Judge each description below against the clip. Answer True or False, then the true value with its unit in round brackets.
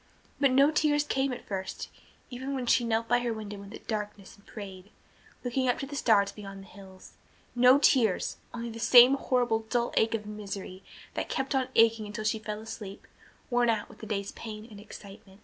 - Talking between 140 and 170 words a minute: False (200 wpm)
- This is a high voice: True (225 Hz)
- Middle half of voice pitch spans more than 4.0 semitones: False (3.2 semitones)